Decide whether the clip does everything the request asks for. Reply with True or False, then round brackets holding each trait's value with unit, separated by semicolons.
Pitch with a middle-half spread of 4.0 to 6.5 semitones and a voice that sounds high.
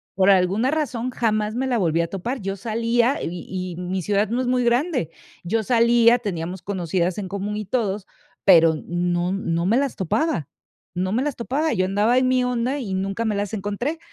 True (4.6 semitones; 210 Hz)